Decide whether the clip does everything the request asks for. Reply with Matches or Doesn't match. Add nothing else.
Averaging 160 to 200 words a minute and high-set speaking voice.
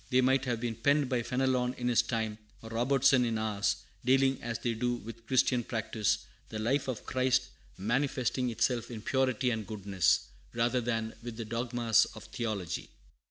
Doesn't match